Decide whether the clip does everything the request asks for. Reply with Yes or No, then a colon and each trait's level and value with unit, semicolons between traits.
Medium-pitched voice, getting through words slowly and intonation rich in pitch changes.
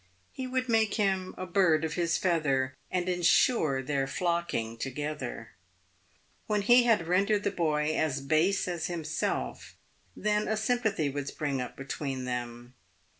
No: medium, 165 Hz; average, 150 wpm; wide, 6.3 semitones